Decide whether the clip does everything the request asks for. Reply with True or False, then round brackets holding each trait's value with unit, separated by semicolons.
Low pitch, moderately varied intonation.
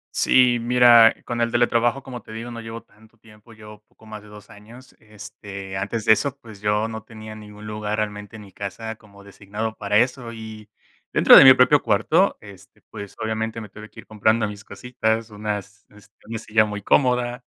False (110 Hz; 1.9 semitones)